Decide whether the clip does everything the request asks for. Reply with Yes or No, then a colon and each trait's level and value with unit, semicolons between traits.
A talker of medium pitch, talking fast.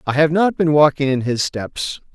Yes: medium, 145 Hz; fast, 225 wpm